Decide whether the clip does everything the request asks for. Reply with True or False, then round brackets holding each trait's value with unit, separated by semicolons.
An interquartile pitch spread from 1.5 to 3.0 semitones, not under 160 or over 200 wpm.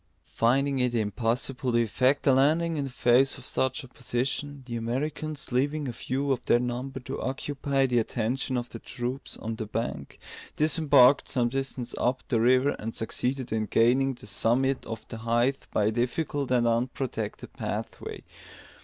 True (2.5 semitones; 165 wpm)